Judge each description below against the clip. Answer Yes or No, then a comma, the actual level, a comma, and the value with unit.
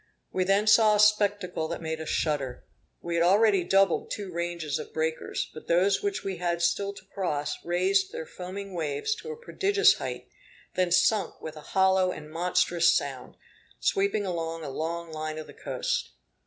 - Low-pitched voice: No, medium, 180 Hz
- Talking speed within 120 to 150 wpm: No, average, 180 wpm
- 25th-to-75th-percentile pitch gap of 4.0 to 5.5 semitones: No, average, 3.6 semitones